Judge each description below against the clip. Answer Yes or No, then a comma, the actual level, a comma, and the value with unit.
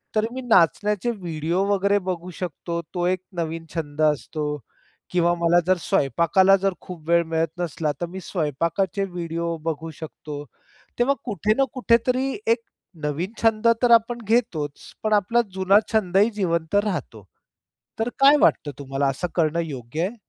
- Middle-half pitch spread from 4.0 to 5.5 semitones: Yes, average, 4.3 semitones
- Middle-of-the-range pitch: Yes, medium, 175 Hz